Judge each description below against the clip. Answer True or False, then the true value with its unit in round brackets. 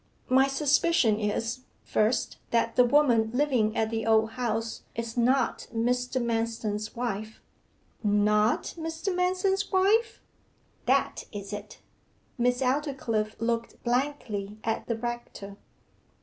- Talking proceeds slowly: True (115 wpm)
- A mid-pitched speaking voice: False (235 Hz)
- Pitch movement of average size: True (3.5 semitones)